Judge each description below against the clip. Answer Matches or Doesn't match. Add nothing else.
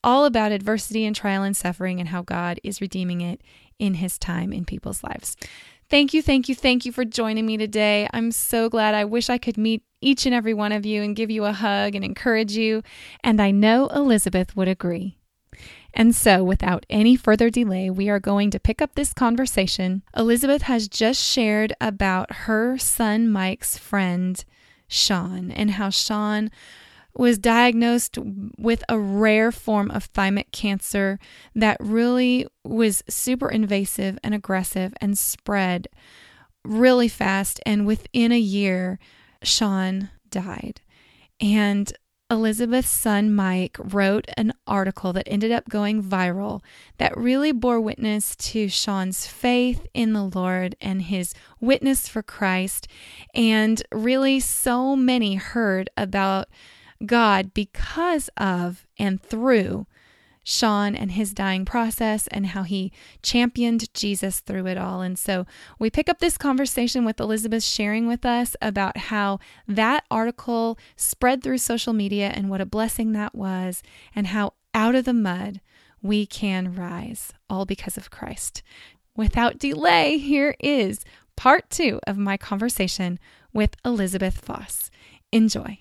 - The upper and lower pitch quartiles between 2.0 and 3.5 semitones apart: Matches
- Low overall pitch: Doesn't match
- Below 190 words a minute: Matches